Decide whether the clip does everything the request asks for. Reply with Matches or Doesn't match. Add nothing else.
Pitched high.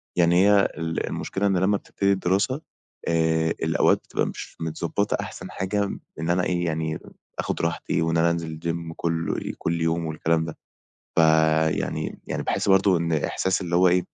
Doesn't match